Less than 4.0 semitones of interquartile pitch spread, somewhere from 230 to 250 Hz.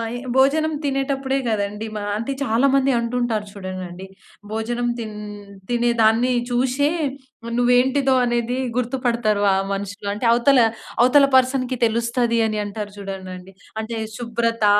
Yes: average, 3.2 semitones; high, 235 Hz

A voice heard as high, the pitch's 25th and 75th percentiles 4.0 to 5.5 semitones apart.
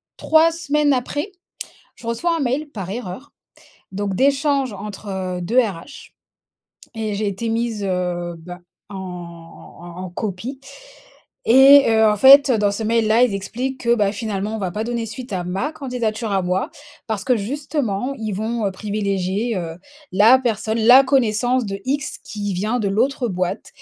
Yes: high, 220 Hz; average, 4.5 semitones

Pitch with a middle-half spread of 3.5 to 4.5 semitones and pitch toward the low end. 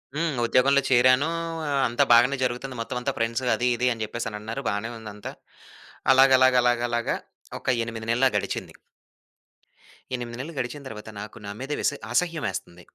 No: narrow, 2.6 semitones; low, 120 Hz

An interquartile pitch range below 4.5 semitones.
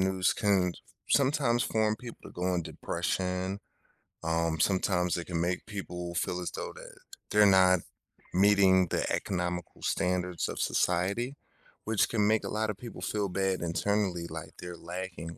Yes: average, 2.8 semitones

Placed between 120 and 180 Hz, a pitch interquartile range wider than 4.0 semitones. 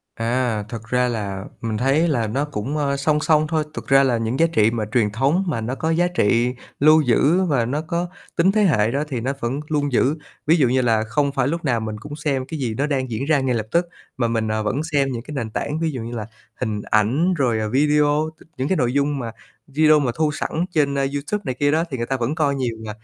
Yes: low, 135 Hz; average, 4.4 semitones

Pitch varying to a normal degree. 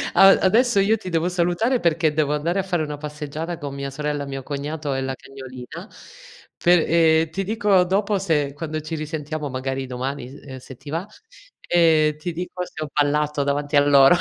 Yes: average, 3.6 semitones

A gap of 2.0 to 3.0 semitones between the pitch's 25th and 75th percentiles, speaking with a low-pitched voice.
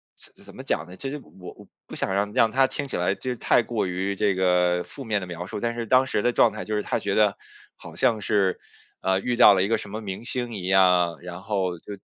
No: average, 3.9 semitones; low, 100 Hz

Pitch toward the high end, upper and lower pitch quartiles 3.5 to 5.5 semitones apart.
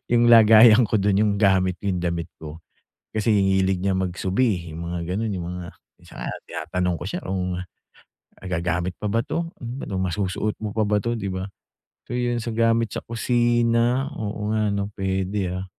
No: low, 100 Hz; average, 3.8 semitones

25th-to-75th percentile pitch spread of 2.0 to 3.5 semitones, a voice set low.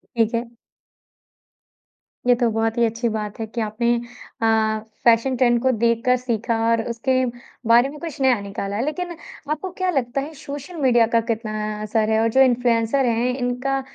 No: narrow, 2.6 semitones; high, 235 Hz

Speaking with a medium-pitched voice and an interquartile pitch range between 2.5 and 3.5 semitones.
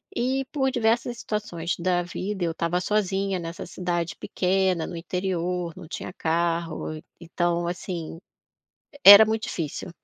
Yes: medium, 180 Hz; average, 3.0 semitones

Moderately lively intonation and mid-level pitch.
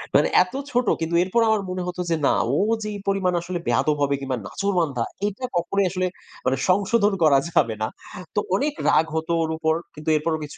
Yes: average, 4.5 semitones; medium, 175 Hz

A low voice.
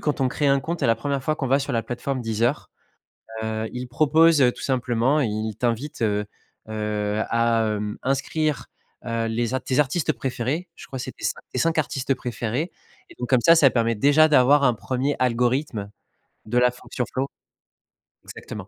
Yes: low, 125 Hz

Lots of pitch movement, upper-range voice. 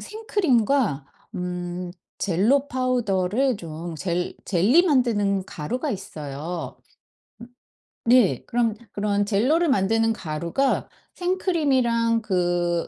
Yes: wide, 6.4 semitones; high, 210 Hz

